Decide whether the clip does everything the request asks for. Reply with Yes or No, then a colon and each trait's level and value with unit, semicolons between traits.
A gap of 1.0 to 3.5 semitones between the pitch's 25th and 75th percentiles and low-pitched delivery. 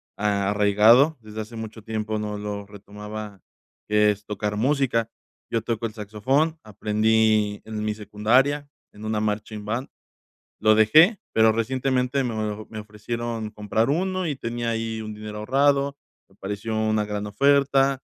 Yes: average, 2.8 semitones; low, 110 Hz